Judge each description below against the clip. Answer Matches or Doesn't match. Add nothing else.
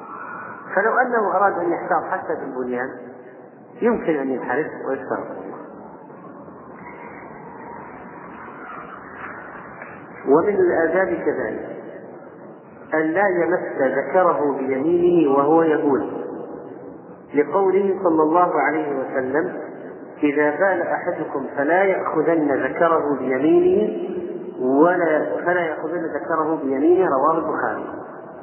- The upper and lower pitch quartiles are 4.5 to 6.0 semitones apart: Matches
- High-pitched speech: Doesn't match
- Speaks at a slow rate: Doesn't match